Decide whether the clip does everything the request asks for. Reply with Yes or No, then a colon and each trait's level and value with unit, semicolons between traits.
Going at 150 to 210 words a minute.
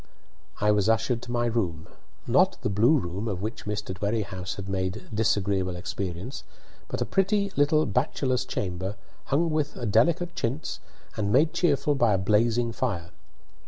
Yes: average, 160 wpm